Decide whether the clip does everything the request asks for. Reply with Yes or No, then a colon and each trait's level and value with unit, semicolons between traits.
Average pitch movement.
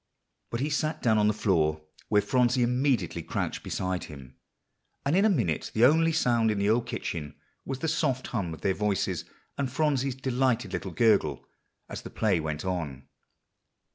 No: wide, 6.7 semitones